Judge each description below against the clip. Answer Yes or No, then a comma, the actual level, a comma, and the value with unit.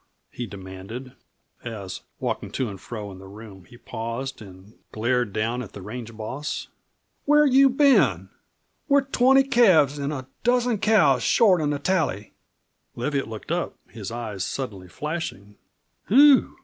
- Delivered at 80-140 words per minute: No, average, 150 wpm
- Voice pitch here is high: No, low, 125 Hz